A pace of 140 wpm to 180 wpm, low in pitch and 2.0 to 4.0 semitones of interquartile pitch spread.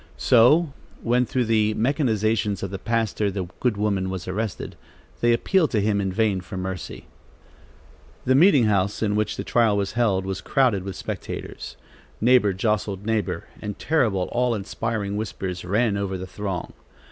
Yes: average, 160 wpm; low, 105 Hz; average, 3.3 semitones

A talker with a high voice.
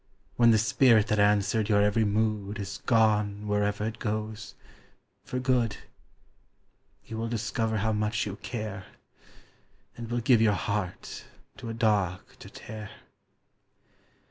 No: low, 105 Hz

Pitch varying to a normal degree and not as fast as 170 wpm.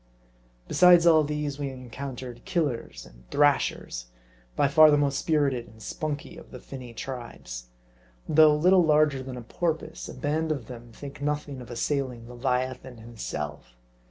Yes: average, 3.9 semitones; average, 150 wpm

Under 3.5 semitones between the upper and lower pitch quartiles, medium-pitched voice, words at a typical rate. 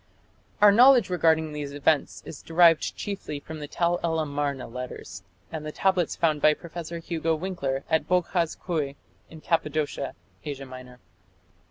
Yes: average, 3.1 semitones; medium, 160 Hz; average, 150 wpm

